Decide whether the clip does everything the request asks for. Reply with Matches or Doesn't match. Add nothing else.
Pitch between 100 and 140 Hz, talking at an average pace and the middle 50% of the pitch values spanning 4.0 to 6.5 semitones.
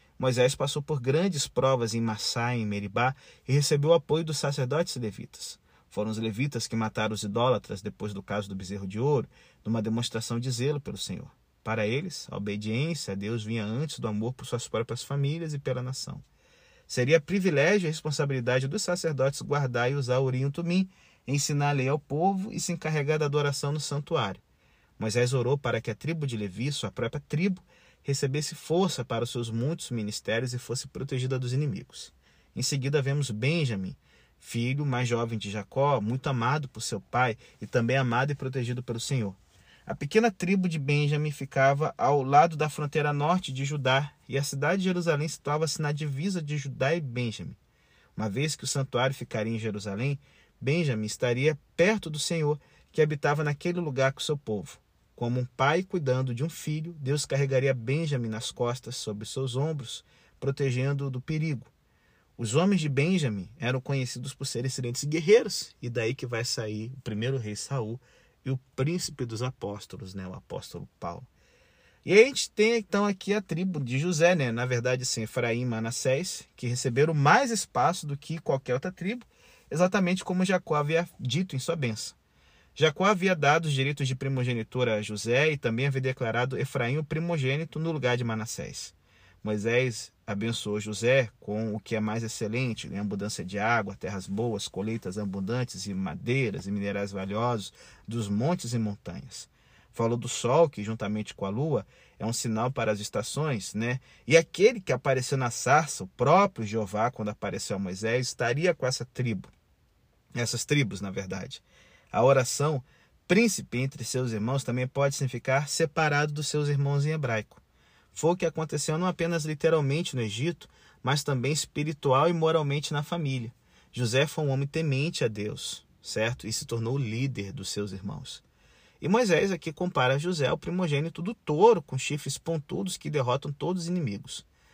Matches